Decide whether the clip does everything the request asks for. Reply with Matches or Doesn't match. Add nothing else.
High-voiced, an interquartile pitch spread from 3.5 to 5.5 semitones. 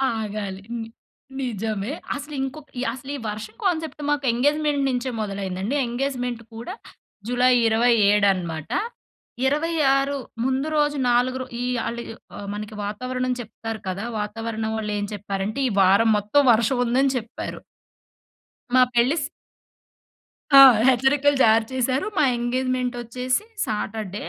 Matches